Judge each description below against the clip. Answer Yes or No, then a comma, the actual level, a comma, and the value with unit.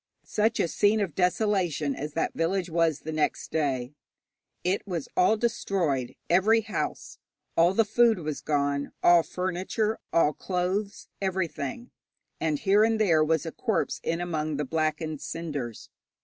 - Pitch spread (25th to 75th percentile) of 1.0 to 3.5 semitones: No, average, 4.5 semitones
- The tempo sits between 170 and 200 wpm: No, average, 145 wpm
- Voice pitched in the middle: Yes, medium, 170 Hz